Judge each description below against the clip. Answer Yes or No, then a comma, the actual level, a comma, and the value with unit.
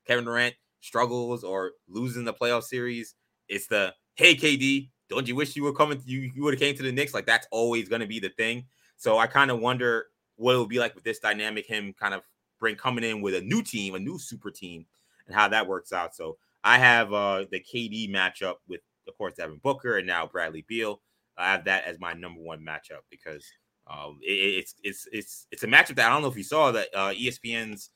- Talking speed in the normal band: No, fast, 235 wpm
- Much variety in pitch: No, average, 3.9 semitones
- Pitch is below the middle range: Yes, low, 115 Hz